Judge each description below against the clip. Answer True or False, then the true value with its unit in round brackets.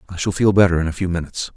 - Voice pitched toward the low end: True (90 Hz)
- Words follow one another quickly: True (310 wpm)